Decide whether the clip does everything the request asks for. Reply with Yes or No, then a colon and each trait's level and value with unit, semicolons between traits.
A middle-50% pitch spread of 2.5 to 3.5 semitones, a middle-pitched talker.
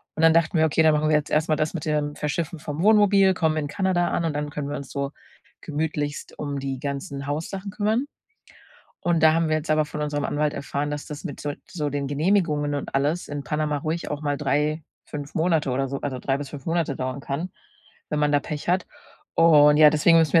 No: narrow, 2.1 semitones; medium, 150 Hz